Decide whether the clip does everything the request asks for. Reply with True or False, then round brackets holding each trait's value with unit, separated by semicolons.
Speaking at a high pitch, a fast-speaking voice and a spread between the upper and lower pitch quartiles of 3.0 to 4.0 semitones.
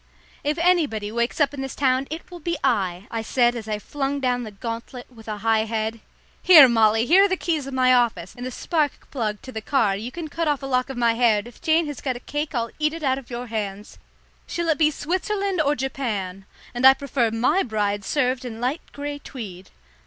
False (255 Hz; 230 wpm; 4.7 semitones)